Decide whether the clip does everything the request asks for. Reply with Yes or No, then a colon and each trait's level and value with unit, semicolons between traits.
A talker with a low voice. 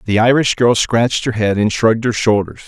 Yes: low, 115 Hz